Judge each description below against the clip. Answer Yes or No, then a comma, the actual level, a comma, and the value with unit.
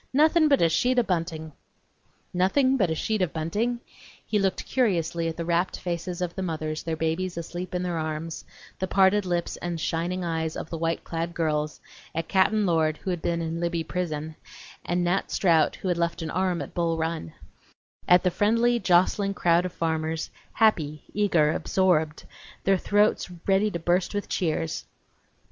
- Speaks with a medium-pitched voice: Yes, medium, 175 Hz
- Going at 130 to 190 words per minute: Yes, average, 180 wpm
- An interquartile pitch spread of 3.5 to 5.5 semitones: No, average, 2.7 semitones